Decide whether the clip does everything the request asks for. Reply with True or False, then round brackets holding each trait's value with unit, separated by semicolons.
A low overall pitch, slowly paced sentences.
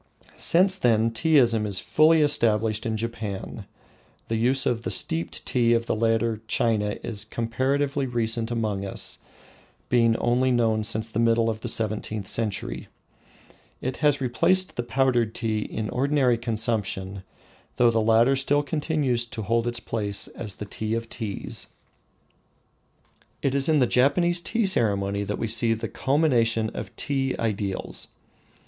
False (115 Hz; 150 wpm)